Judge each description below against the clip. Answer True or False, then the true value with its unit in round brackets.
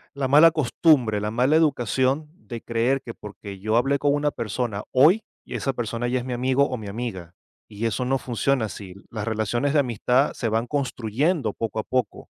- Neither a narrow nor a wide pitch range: True (3.9 semitones)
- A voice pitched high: False (120 Hz)